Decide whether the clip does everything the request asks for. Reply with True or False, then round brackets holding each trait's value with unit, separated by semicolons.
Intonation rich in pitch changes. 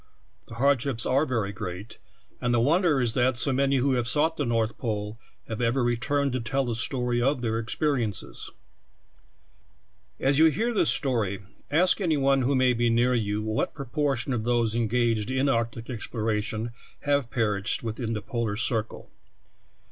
False (3.4 semitones)